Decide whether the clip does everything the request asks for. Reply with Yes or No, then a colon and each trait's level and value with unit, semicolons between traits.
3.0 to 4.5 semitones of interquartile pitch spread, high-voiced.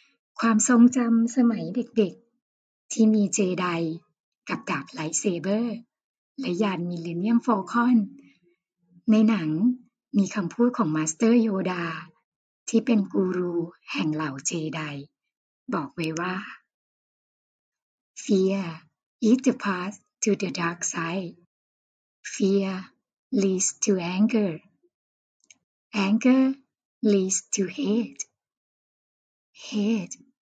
No: average, 4.9 semitones; high, 200 Hz